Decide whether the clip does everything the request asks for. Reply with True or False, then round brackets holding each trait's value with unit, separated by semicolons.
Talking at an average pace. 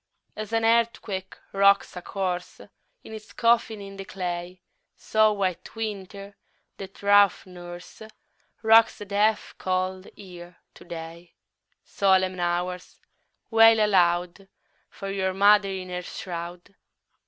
False (130 wpm)